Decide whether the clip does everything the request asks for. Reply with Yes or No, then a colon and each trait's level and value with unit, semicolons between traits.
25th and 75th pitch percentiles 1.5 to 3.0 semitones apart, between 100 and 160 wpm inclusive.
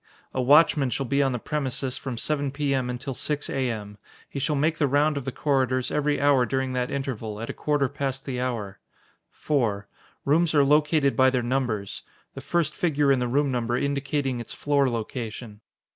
No: average, 2.7 semitones; average, 190 wpm